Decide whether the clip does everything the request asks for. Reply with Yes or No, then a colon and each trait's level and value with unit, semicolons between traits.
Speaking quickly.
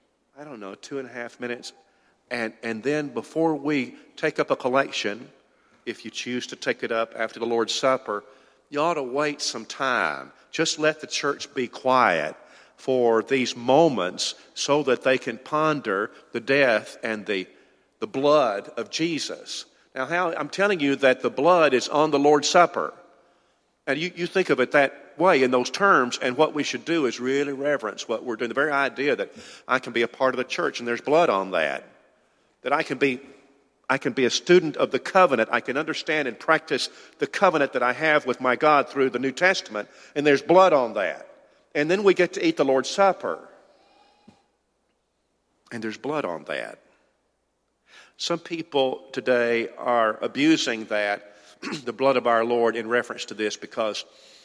No: average, 190 wpm